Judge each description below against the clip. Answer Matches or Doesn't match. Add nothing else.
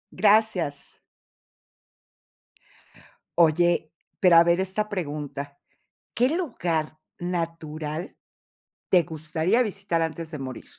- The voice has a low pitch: Doesn't match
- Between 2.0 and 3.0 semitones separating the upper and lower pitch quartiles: Doesn't match